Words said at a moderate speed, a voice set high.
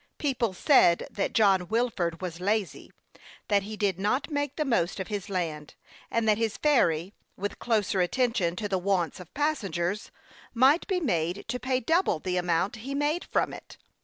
Yes: average, 180 wpm; high, 205 Hz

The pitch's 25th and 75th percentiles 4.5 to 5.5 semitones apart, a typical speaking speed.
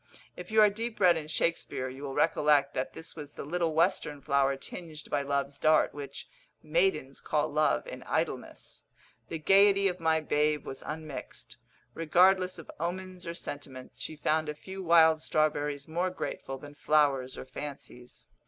No: average, 3.7 semitones; average, 165 wpm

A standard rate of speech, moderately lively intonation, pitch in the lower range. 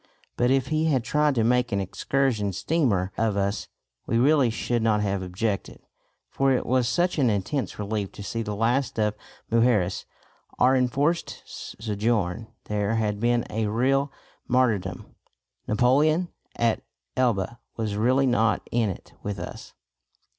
Yes: average, 145 wpm; average, 3.8 semitones; low, 115 Hz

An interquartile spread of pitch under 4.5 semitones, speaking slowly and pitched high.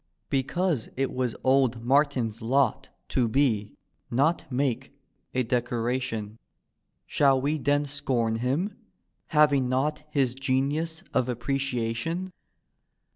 No: average, 3.0 semitones; slow, 105 wpm; low, 130 Hz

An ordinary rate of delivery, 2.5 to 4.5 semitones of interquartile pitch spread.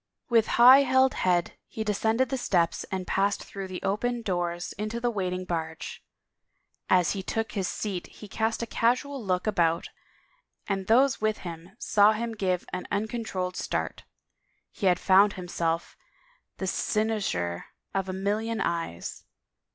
Yes: average, 150 wpm; average, 3.6 semitones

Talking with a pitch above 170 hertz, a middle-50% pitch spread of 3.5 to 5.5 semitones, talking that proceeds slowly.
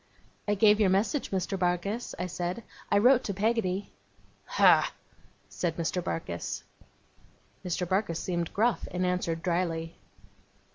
No: medium, 185 Hz; average, 3.1 semitones; slow, 130 wpm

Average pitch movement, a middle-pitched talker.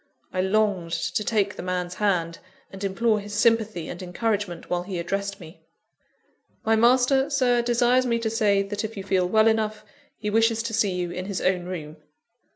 No: average, 3.6 semitones; high, 205 Hz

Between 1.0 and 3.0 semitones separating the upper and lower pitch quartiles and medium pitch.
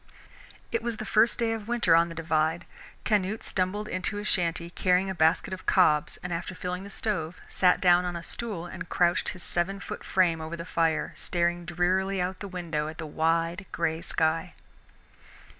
Yes: narrow, 2.4 semitones; medium, 180 Hz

